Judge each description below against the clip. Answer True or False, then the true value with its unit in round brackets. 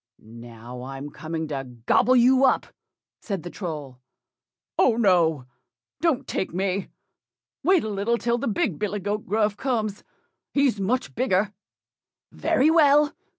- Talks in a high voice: True (205 Hz)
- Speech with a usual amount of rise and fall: False (7.6 semitones)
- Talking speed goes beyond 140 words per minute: False (135 wpm)